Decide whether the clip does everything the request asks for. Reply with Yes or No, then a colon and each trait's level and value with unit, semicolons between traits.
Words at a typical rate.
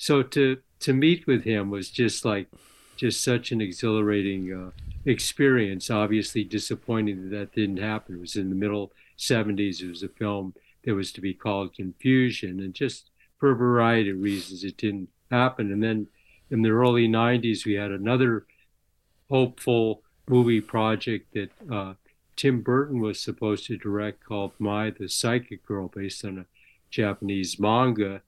Yes: average, 165 wpm